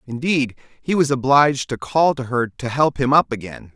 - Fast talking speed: Yes, fast, 210 wpm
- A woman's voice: No, male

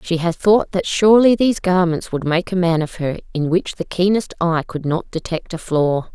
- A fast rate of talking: Yes, fast, 225 wpm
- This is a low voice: No, medium, 175 Hz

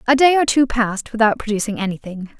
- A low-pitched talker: No, high, 230 Hz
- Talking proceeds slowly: No, average, 200 wpm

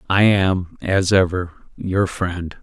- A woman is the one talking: No, male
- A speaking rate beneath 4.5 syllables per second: Yes, 3.4 syllables/s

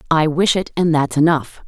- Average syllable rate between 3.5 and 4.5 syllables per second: No, 5.1 syllables/s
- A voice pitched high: No, medium, 155 Hz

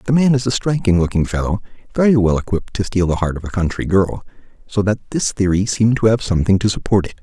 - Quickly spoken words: Yes, fast, 240 wpm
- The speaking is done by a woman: No, male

